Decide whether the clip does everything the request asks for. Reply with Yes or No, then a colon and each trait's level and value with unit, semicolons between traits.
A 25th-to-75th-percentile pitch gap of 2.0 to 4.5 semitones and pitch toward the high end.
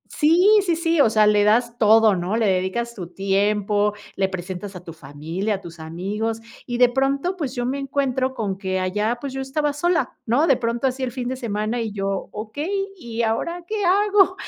No: wide, 5.5 semitones; high, 230 Hz